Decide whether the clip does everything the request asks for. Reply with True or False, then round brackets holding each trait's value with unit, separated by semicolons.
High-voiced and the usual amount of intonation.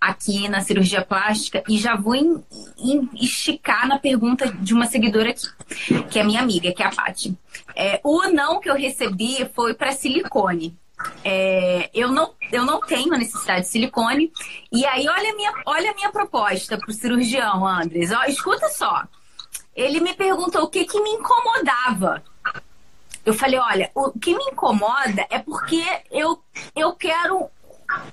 False (255 Hz; 7.1 semitones)